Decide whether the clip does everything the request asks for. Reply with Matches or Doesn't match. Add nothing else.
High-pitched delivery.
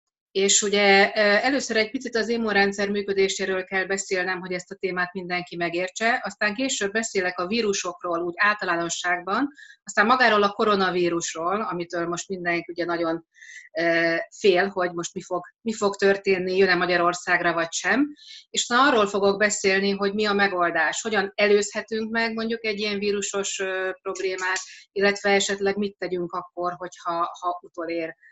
Matches